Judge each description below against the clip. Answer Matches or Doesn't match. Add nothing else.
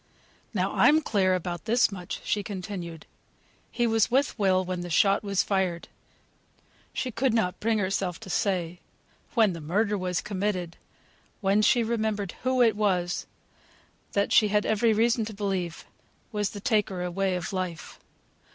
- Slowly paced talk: Doesn't match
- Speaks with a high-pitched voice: Matches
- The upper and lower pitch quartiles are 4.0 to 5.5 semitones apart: Doesn't match